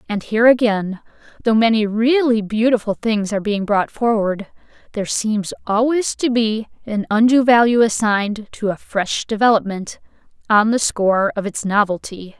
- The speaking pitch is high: Yes, high, 215 Hz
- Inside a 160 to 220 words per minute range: No, average, 150 wpm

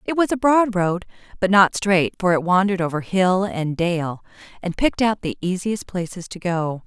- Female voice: Yes, female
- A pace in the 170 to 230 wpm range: Yes, average, 200 wpm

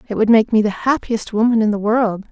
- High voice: Yes, high, 220 Hz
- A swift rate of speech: Yes, fast, 260 wpm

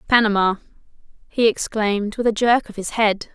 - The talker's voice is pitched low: No, high, 215 Hz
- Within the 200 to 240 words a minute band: No, average, 160 wpm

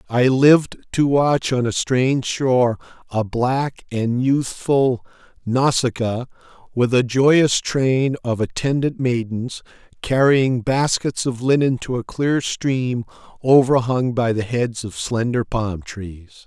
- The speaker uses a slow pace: Yes, slow, 130 wpm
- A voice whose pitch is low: Yes, low, 125 Hz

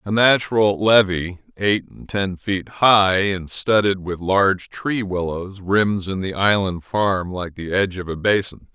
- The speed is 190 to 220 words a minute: No, average, 170 wpm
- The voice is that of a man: Yes, male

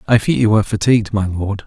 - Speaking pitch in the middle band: No, low, 105 Hz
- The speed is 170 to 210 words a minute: No, fast, 250 wpm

